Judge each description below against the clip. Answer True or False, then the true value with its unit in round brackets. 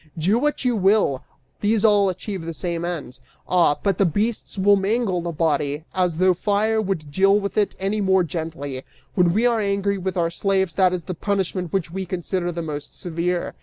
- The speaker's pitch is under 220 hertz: True (185 Hz)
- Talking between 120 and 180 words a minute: False (200 wpm)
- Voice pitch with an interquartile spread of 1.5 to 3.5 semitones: True (3.0 semitones)